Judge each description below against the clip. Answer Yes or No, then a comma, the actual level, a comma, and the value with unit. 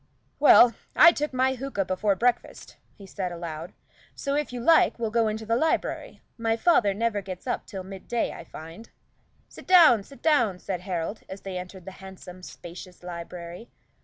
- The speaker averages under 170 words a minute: No, average, 175 wpm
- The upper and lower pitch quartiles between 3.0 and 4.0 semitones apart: No, average, 5.0 semitones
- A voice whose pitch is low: No, high, 200 Hz